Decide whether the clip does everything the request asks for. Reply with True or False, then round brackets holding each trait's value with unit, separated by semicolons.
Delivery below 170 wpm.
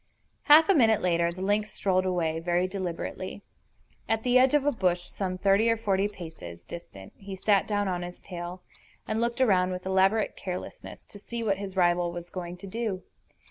False (190 wpm)